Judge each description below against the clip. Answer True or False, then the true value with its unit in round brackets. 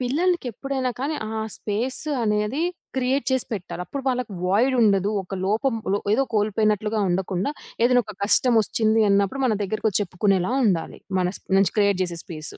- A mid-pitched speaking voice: False (215 Hz)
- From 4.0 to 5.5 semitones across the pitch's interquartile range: True (4.3 semitones)